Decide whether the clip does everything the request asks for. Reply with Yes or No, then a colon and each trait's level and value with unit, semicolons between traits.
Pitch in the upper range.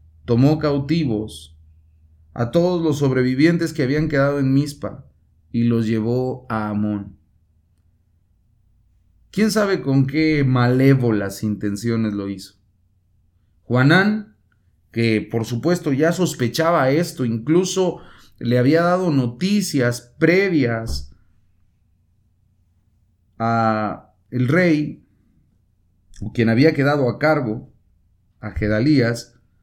No: low, 115 Hz